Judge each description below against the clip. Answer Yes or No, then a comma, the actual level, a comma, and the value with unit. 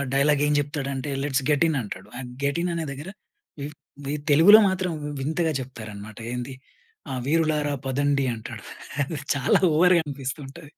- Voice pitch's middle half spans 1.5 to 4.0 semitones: Yes, average, 2.9 semitones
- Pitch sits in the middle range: Yes, medium, 145 Hz